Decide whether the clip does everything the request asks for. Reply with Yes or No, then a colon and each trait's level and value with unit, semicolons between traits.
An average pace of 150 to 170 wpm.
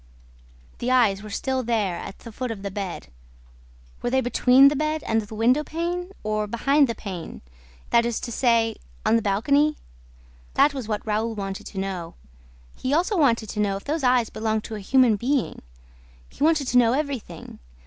No: average, 190 wpm